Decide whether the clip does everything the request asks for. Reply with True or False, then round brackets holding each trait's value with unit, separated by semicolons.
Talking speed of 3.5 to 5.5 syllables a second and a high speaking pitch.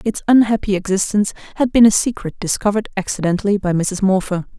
False (6.4 syllables/s; 200 Hz)